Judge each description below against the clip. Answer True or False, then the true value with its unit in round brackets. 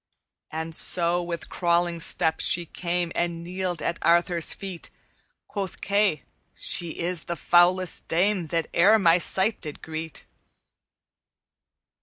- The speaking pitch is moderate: True (175 Hz)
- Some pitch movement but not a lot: False (1.6 semitones)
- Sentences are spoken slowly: True (125 wpm)